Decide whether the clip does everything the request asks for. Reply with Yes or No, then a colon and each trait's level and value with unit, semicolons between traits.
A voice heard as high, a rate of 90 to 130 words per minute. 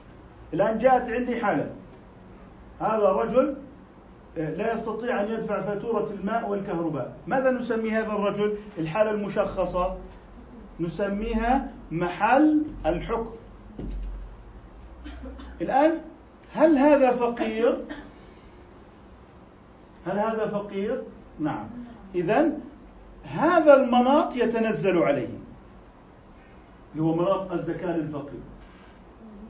No: high, 215 Hz; average, 80 wpm